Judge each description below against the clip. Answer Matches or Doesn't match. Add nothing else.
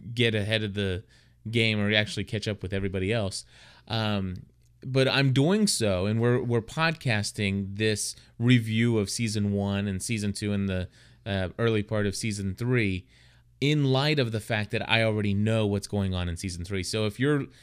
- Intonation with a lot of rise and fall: Doesn't match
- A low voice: Matches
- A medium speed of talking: Matches